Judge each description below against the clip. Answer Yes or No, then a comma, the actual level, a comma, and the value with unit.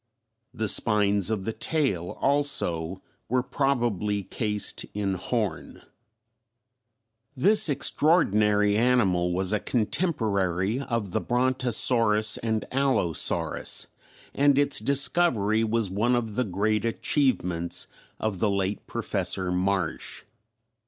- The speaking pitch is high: No, low, 110 Hz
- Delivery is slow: Yes, slow, 105 wpm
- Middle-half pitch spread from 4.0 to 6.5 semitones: Yes, average, 4.4 semitones